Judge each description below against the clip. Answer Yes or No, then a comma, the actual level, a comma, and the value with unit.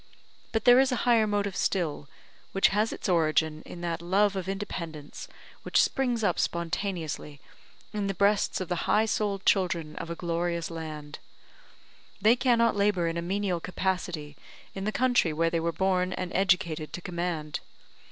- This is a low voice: No, medium, 180 Hz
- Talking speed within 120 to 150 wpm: No, average, 165 wpm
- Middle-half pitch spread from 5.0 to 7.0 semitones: No, average, 3.4 semitones